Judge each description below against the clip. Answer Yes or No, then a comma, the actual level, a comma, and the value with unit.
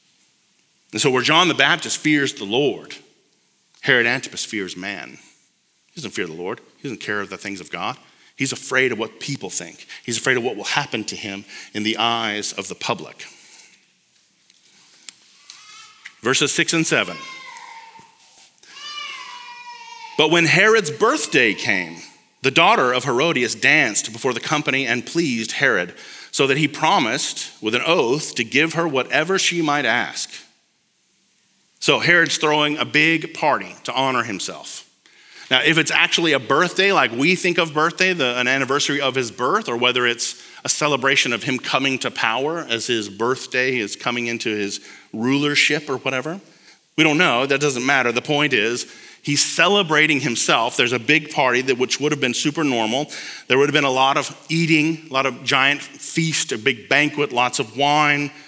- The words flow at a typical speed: Yes, average, 170 wpm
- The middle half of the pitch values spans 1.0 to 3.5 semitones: No, average, 4.6 semitones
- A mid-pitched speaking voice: Yes, medium, 145 Hz